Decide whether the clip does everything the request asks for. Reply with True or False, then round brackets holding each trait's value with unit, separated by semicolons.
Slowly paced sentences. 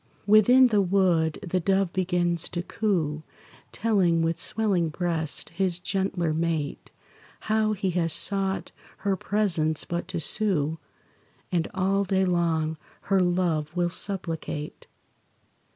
True (120 wpm)